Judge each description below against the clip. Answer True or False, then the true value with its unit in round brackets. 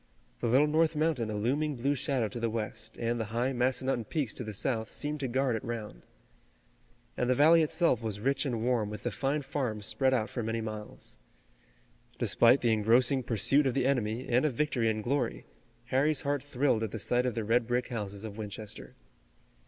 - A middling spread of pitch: True (3.6 semitones)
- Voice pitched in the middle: False (120 Hz)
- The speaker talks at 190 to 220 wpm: True (200 wpm)